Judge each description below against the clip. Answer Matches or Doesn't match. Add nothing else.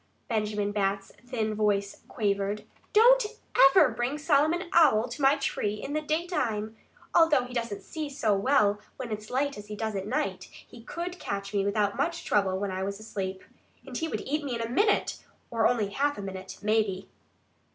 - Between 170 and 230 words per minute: Matches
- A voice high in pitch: Matches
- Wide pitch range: Matches